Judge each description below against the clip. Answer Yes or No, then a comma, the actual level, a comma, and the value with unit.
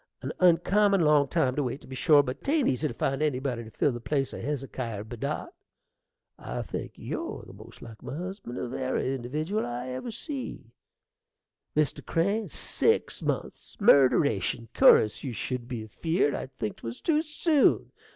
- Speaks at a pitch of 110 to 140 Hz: Yes, low, 135 Hz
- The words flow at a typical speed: Yes, average, 165 wpm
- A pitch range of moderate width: No, wide, 5.9 semitones